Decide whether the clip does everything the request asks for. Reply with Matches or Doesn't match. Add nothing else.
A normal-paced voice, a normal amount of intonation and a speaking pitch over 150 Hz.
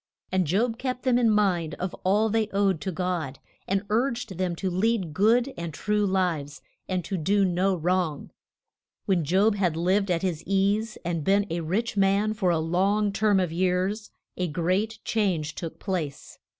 Matches